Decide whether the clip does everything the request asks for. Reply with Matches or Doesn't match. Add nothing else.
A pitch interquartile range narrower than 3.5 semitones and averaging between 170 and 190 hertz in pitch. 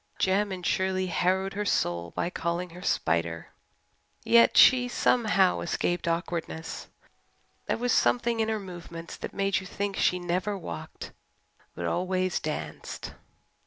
Matches